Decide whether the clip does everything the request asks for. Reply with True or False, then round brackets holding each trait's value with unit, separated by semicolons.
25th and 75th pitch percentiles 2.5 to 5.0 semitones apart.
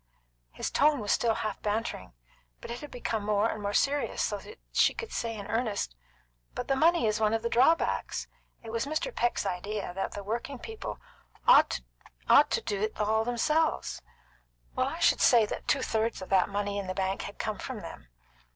True (4.1 semitones)